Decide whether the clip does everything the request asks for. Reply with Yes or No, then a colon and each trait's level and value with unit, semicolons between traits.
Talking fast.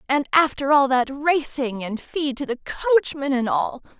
No: average, 180 wpm